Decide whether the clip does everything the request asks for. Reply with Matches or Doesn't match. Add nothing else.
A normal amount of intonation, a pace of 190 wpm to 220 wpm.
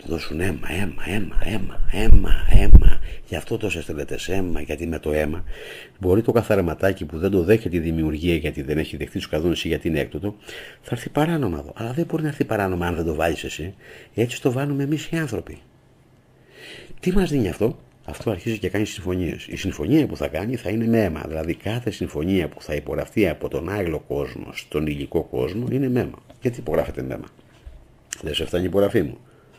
Doesn't match